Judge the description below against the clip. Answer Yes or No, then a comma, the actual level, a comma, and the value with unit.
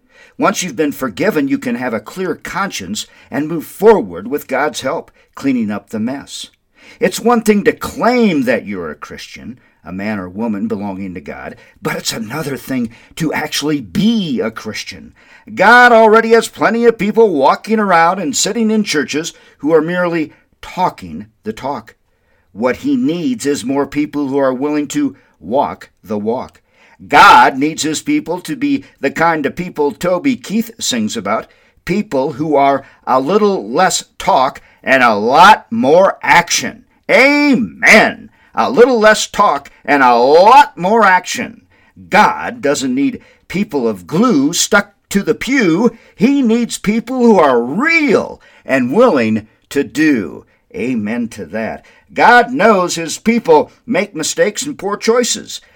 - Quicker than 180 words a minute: No, average, 155 wpm